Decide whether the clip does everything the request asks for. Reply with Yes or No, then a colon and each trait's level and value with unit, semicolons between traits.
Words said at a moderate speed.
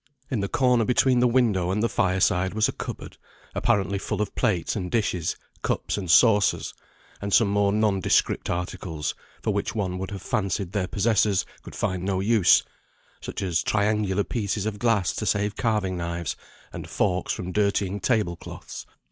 Yes: average, 175 wpm